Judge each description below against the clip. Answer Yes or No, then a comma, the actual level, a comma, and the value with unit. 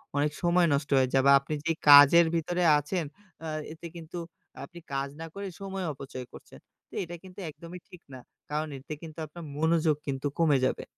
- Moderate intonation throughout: Yes, average, 3.2 semitones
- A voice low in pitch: No, medium, 160 Hz